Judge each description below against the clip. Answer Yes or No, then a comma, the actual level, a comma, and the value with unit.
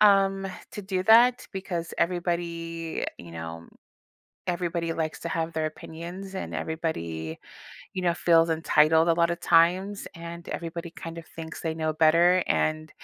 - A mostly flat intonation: Yes, narrow, 1.9 semitones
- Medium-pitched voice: Yes, medium, 170 Hz